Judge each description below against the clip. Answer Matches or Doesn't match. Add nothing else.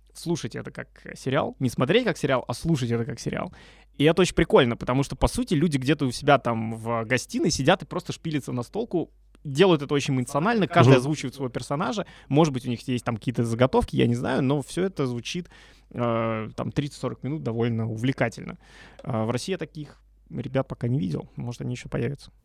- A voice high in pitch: Doesn't match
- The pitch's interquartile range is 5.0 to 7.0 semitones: Doesn't match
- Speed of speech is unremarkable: Doesn't match